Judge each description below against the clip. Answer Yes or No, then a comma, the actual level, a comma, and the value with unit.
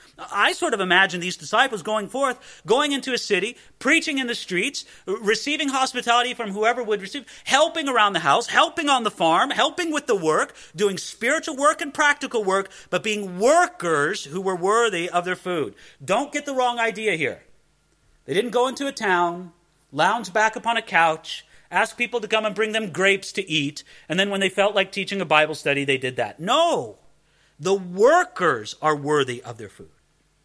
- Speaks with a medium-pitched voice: No, high, 210 Hz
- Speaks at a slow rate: No, average, 190 wpm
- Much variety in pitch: Yes, wide, 6.0 semitones